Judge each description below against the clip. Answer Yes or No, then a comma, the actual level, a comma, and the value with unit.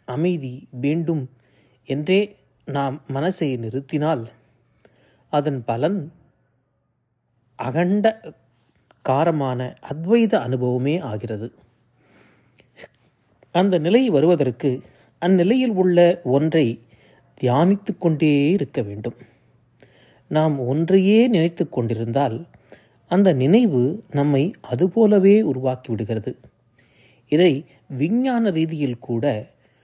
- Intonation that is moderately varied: No, wide, 5.8 semitones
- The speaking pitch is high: No, medium, 140 Hz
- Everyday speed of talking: No, slow, 70 wpm